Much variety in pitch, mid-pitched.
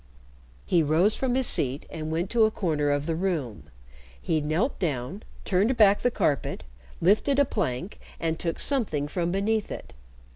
Yes: wide, 5.9 semitones; medium, 175 Hz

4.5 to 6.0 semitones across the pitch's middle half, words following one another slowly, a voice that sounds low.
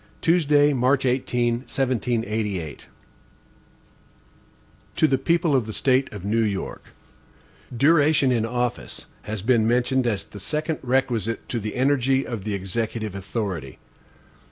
No: average, 3.7 semitones; slow, 130 wpm; low, 120 Hz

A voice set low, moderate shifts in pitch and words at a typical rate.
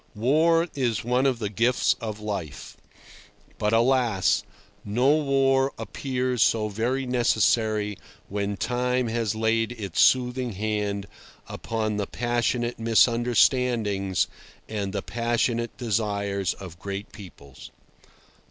No: low, 115 Hz; average, 3.3 semitones; slow, 110 wpm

